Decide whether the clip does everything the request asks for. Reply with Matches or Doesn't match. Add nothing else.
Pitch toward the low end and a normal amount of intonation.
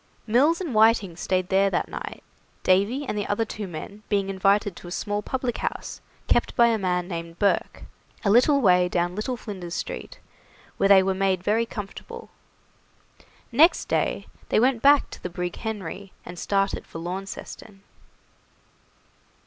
Doesn't match